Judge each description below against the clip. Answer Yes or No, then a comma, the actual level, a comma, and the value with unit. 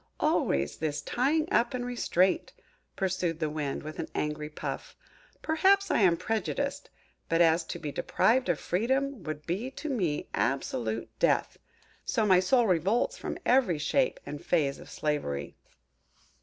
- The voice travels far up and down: Yes, wide, 8.4 semitones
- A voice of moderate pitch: Yes, medium, 180 Hz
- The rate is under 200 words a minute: Yes, average, 150 wpm